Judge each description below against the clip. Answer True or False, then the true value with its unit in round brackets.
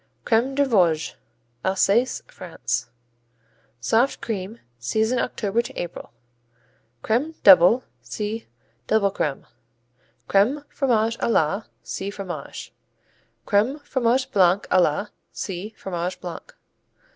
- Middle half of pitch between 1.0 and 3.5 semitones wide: False (4.5 semitones)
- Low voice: False (210 Hz)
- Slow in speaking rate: True (105 wpm)